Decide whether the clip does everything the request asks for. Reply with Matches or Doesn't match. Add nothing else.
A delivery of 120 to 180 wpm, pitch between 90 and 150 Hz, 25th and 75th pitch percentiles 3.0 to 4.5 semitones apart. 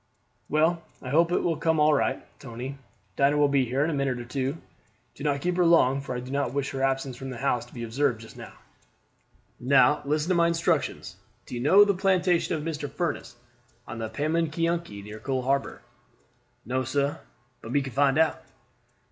Doesn't match